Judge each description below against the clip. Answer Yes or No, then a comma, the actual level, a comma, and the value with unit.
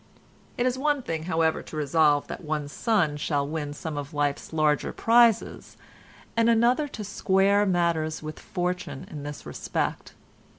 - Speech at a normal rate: Yes, average, 155 wpm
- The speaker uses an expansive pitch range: Yes, wide, 5.8 semitones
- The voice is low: No, medium, 160 Hz